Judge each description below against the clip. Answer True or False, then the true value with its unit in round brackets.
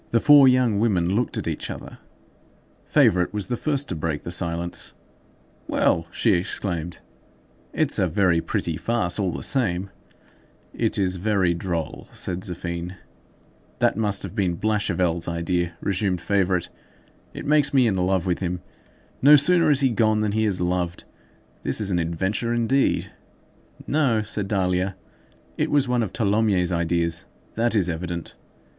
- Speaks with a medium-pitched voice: False (95 Hz)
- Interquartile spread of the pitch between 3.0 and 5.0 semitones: True (4.3 semitones)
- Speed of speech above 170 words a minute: False (155 wpm)